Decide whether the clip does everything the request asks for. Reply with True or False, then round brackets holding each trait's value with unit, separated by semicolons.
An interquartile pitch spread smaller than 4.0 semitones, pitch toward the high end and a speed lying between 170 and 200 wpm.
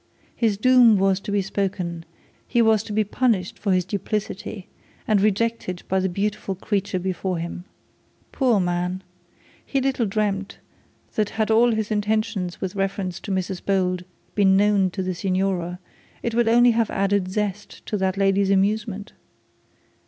False (2.4 semitones; 200 Hz; 155 wpm)